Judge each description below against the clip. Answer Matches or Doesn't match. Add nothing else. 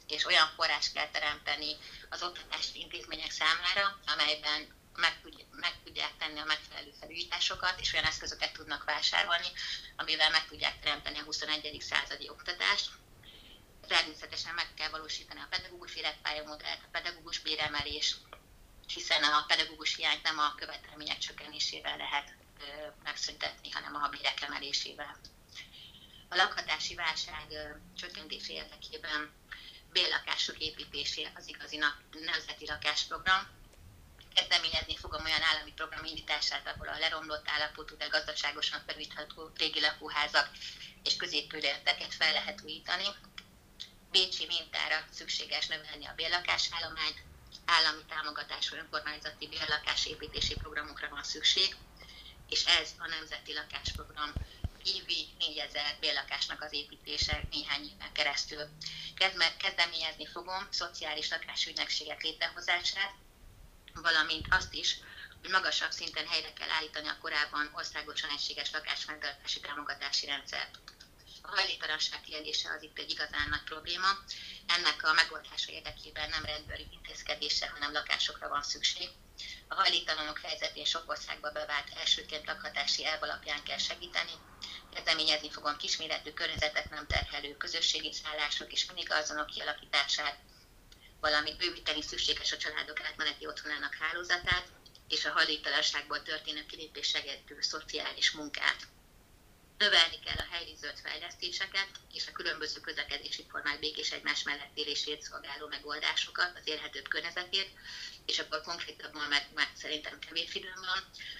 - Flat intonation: Matches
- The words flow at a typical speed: Matches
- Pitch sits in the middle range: Matches